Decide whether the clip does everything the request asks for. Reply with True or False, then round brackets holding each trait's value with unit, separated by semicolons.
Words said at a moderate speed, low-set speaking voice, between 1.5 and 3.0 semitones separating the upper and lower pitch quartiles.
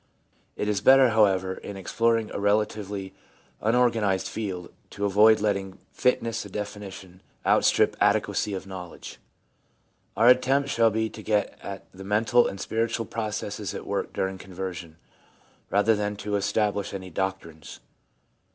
True (145 wpm; 105 Hz; 2.6 semitones)